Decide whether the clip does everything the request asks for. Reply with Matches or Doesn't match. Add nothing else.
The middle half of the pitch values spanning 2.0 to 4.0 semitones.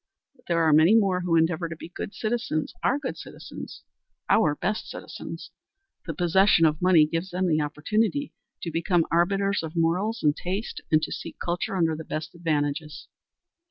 Matches